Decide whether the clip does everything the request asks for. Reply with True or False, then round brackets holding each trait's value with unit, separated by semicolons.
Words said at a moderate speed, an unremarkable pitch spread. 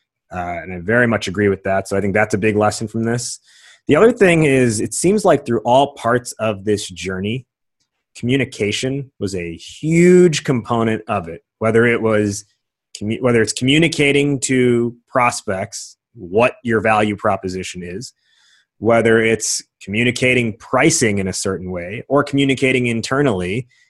True (155 wpm; 4.0 semitones)